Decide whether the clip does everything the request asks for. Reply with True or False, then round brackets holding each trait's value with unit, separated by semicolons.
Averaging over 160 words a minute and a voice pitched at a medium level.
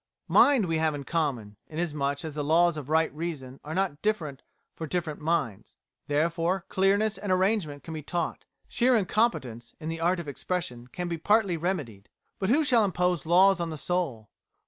True (180 wpm; 165 Hz)